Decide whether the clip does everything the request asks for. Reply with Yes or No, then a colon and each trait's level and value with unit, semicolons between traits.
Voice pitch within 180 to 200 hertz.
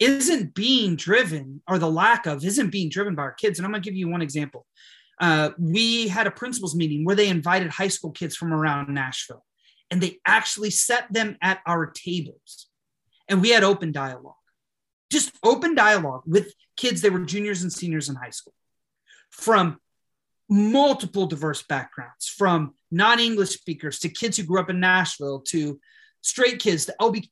Yes: medium, 185 Hz